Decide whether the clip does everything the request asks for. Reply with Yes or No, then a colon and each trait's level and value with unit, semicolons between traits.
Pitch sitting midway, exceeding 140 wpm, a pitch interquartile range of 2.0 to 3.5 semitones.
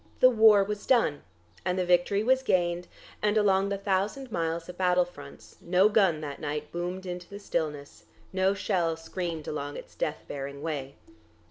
No: medium, 180 Hz; average, 170 wpm; average, 3.9 semitones